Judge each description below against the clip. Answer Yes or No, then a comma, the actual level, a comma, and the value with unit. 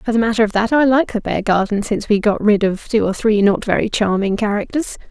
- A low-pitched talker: No, high, 215 Hz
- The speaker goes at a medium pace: No, fast, 245 wpm